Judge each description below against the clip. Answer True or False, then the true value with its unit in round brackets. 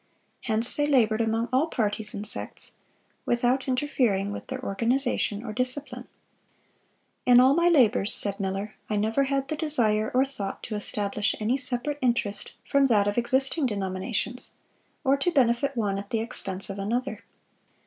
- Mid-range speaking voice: False (240 Hz)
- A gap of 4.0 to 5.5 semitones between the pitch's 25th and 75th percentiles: True (4.3 semitones)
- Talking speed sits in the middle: True (160 wpm)